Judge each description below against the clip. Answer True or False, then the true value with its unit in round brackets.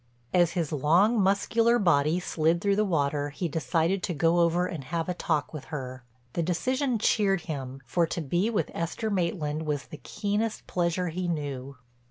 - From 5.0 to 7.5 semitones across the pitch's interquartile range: False (4.3 semitones)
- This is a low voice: False (170 Hz)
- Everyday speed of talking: True (180 wpm)